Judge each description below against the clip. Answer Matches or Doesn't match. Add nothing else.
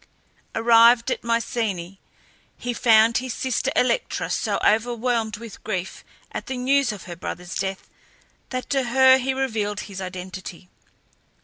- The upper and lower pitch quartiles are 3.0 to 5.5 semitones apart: Matches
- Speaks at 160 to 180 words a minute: Doesn't match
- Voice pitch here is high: Matches